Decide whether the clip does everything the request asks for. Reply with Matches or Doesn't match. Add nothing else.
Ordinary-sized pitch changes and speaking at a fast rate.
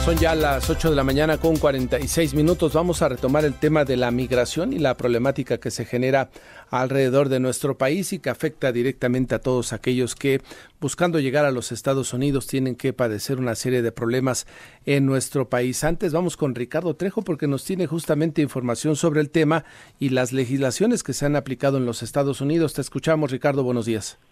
Matches